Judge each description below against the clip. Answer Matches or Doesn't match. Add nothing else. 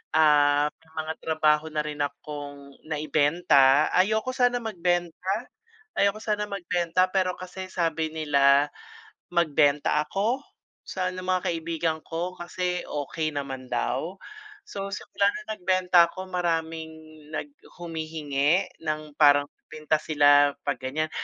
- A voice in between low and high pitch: Matches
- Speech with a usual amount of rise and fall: Matches